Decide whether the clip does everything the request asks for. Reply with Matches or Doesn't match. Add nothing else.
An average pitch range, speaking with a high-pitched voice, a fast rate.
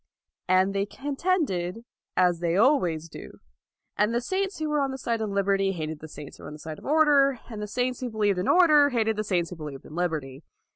Doesn't match